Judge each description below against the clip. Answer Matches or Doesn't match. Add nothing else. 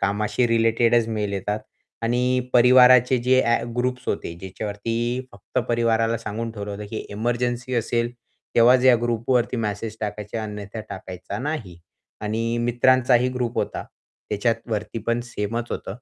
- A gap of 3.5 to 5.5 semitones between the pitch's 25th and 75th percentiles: Doesn't match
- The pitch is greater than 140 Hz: Doesn't match